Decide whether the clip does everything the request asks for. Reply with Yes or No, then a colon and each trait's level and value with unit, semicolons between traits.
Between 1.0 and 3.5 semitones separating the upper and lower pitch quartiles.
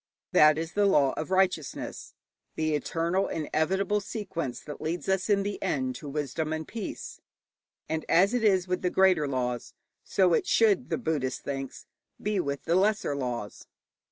No: average, 4.7 semitones